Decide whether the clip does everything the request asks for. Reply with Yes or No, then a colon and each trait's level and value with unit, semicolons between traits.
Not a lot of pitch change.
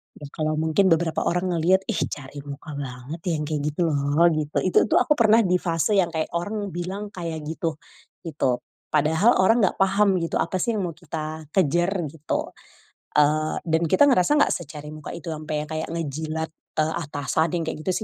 No: average, 3.3 semitones